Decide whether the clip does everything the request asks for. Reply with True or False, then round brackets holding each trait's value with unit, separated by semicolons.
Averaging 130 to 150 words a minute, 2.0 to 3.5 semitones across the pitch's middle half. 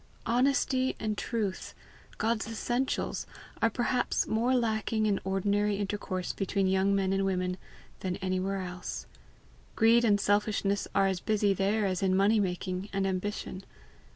True (140 wpm; 2.5 semitones)